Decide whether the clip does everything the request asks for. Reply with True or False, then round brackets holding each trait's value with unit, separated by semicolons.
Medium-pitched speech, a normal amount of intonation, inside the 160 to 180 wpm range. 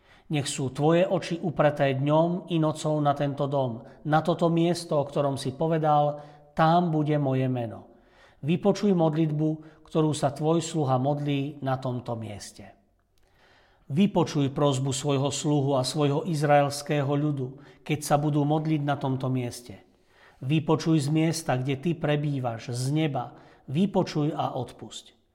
False (145 Hz; 3.1 semitones; 135 wpm)